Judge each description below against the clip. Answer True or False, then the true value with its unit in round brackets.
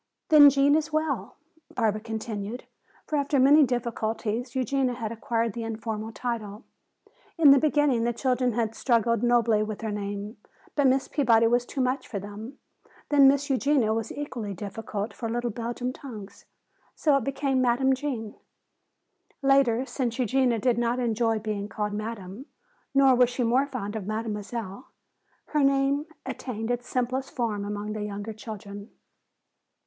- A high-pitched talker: True (235 Hz)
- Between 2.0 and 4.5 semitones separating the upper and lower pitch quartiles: True (3.6 semitones)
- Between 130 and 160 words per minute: True (155 wpm)